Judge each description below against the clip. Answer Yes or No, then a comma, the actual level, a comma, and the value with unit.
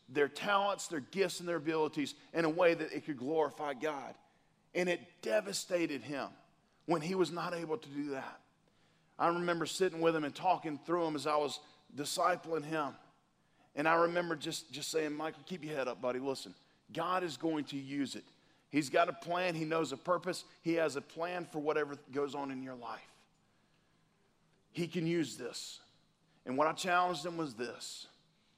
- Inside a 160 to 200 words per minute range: Yes, average, 190 wpm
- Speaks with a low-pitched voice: No, medium, 160 Hz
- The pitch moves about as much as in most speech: Yes, average, 3.1 semitones